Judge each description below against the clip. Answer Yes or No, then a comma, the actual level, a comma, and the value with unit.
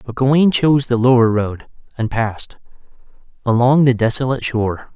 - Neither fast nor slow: Yes, average, 145 wpm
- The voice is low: Yes, low, 125 Hz